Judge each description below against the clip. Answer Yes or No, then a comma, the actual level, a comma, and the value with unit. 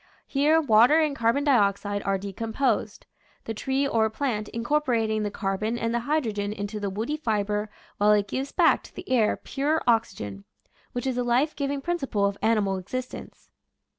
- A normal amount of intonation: Yes, average, 4.7 semitones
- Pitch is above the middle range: Yes, high, 230 Hz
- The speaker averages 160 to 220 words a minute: Yes, average, 170 wpm